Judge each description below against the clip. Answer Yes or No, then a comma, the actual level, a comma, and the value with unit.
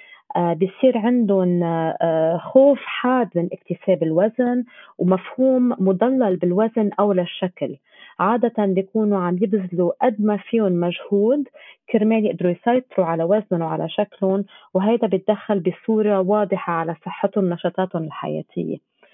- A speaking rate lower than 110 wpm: No, average, 115 wpm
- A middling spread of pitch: Yes, average, 4.0 semitones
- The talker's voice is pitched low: No, high, 195 Hz